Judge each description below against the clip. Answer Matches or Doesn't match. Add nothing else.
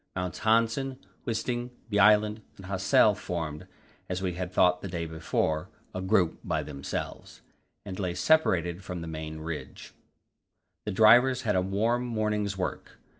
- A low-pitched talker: Matches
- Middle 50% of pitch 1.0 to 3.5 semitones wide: Doesn't match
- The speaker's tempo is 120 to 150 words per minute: Matches